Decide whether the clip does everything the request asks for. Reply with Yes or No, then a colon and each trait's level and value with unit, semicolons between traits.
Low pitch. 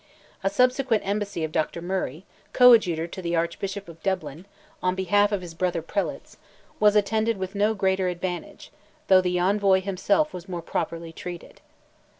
No: high, 190 Hz